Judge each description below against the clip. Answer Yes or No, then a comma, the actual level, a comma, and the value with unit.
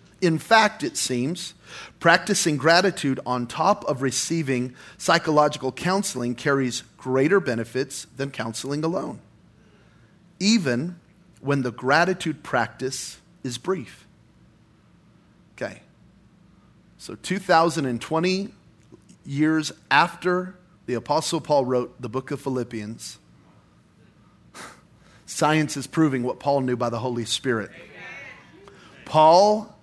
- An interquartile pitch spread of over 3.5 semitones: Yes, wide, 5.4 semitones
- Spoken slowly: Yes, slow, 100 wpm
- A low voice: No, medium, 150 Hz